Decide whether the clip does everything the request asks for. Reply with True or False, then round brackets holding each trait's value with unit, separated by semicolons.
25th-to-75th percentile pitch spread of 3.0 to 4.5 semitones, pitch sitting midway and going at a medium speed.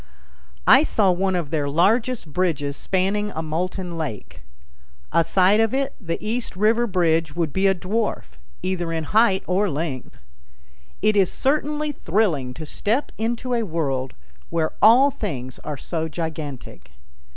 False (5.5 semitones; 180 Hz; 145 wpm)